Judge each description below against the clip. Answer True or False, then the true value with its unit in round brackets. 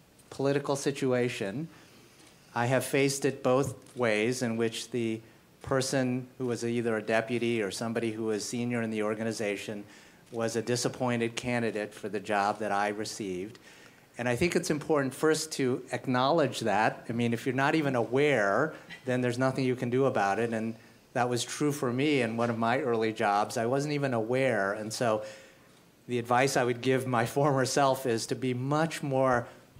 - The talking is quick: False (180 wpm)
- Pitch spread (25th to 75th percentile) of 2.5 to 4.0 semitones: True (2.9 semitones)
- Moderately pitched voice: False (120 Hz)